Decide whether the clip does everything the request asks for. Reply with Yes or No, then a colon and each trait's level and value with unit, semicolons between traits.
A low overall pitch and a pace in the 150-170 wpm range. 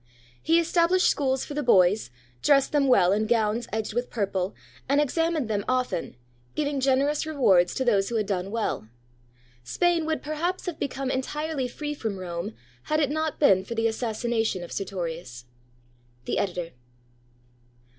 No: high, 245 Hz; average, 155 wpm